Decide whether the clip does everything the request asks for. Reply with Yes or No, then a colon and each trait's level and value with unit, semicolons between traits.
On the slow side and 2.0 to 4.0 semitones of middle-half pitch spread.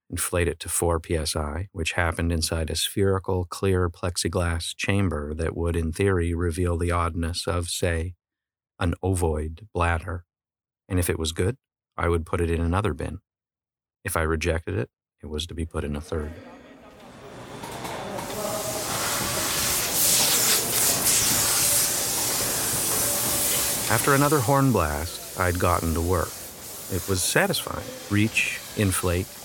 Yes: slow, 125 wpm; narrow, 2.6 semitones